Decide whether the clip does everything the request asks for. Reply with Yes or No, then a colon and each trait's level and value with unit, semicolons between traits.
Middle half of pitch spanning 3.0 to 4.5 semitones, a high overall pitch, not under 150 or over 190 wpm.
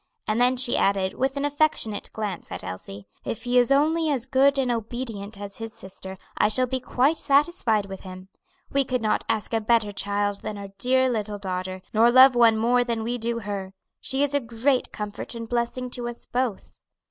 No: average, 4.0 semitones; high, 230 Hz; fast, 205 wpm